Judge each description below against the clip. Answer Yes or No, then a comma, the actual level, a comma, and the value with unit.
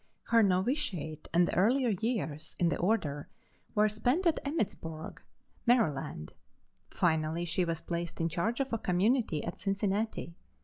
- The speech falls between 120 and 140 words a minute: Yes, slow, 135 wpm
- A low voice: No, medium, 185 Hz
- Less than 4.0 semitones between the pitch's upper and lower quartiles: No, wide, 5.6 semitones